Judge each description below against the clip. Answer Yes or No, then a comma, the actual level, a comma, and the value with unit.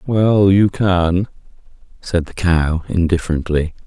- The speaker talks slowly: Yes, slow, 110 wpm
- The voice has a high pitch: No, very low, 90 Hz